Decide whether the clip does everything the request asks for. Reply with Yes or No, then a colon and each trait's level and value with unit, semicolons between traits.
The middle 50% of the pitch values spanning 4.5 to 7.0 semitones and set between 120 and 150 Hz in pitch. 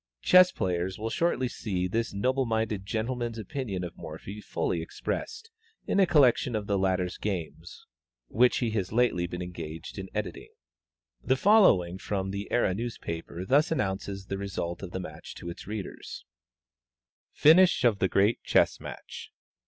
No: average, 4.9 semitones; low, 100 Hz